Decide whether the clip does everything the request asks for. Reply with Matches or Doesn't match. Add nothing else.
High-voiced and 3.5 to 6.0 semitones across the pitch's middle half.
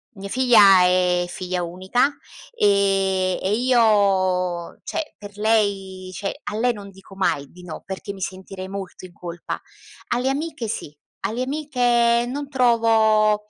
Matches